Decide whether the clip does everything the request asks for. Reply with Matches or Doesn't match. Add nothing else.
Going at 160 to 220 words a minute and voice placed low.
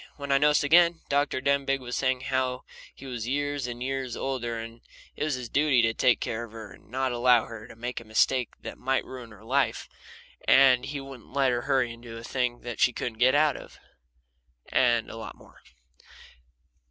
Matches